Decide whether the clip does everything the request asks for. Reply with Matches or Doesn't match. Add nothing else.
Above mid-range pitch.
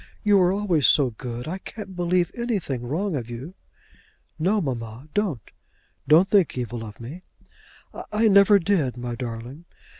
Doesn't match